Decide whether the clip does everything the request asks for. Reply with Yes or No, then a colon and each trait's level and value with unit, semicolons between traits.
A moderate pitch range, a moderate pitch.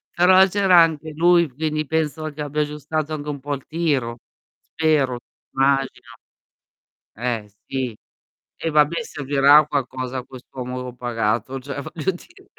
Yes: average, 3.5 semitones; medium, 145 Hz